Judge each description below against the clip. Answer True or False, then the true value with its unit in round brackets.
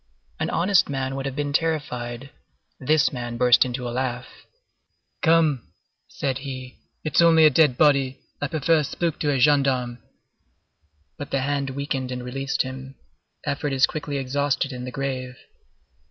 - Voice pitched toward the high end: False (135 Hz)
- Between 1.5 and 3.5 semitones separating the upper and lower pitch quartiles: True (2.4 semitones)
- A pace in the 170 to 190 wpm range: False (155 wpm)